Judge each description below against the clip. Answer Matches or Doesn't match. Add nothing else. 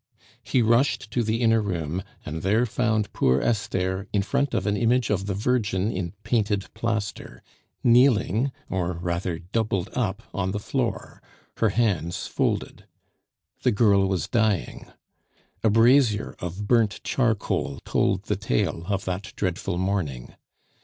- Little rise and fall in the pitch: Doesn't match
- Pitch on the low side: Matches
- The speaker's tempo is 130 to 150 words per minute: Matches